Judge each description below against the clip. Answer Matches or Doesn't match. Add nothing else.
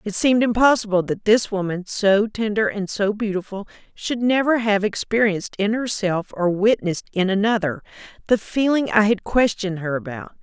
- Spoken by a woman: Matches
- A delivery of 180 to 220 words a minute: Doesn't match